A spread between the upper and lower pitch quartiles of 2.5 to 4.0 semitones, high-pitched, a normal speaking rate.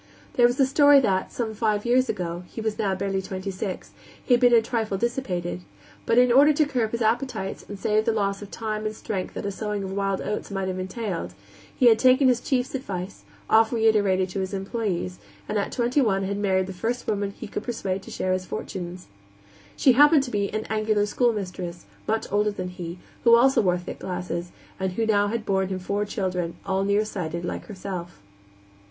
No: average, 3.6 semitones; high, 205 Hz; fast, 210 wpm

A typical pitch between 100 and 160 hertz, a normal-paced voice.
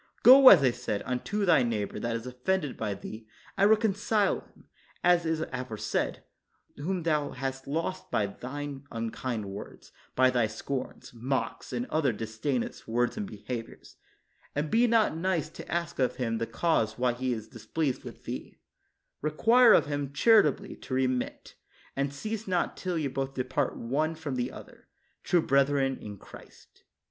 Yes: medium, 140 Hz; average, 160 wpm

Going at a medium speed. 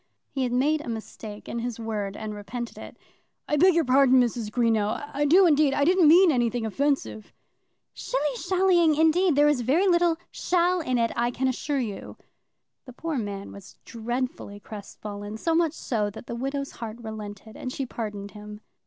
Yes: average, 180 wpm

